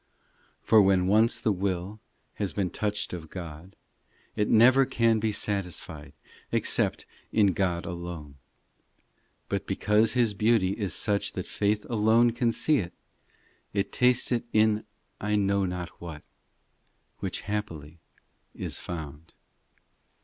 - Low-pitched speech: Yes, low, 100 Hz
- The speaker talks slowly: Yes, slow, 130 wpm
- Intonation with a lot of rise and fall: No, average, 3.7 semitones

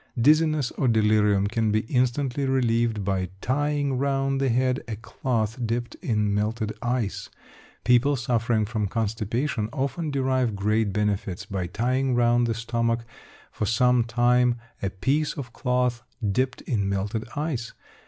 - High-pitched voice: No, low, 120 Hz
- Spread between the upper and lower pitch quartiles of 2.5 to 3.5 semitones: Yes, average, 3.2 semitones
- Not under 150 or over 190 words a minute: No, average, 140 wpm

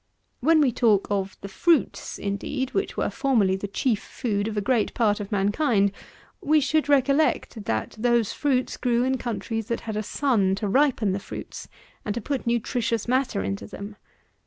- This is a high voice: Yes, high, 230 Hz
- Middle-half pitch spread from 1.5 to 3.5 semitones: No, average, 4.6 semitones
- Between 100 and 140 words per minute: No, average, 180 wpm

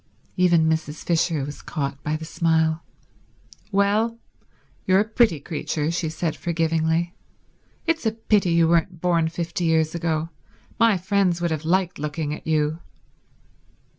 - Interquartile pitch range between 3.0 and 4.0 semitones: No, narrow, 2.4 semitones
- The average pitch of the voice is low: No, medium, 165 Hz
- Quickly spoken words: No, average, 140 wpm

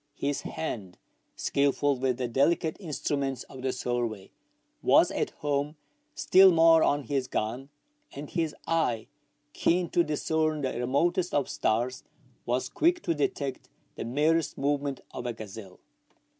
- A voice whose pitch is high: No, medium, 140 Hz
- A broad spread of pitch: No, average, 4.3 semitones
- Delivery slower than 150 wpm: Yes, average, 140 wpm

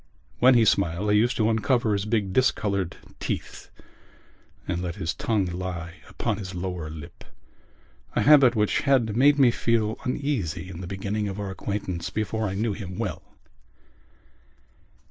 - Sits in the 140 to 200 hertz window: No, low, 105 Hz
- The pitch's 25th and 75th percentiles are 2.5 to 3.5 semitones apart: No, average, 3.9 semitones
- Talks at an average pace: Yes, average, 150 wpm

